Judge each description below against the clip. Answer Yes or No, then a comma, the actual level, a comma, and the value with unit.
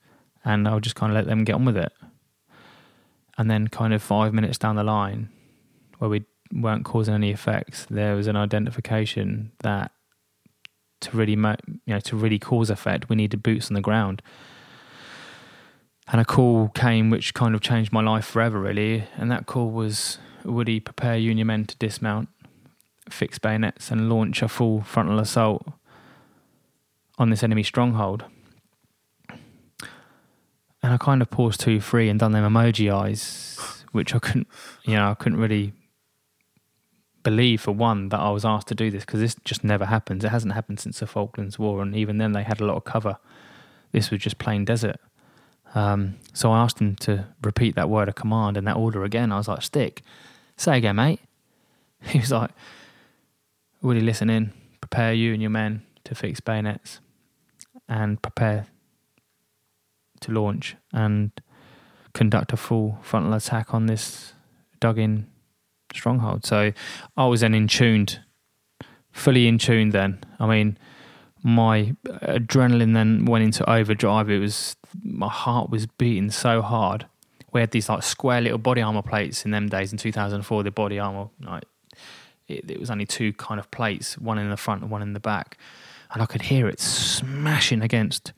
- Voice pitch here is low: Yes, low, 110 Hz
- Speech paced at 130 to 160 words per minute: No, average, 175 wpm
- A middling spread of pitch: No, narrow, 1.7 semitones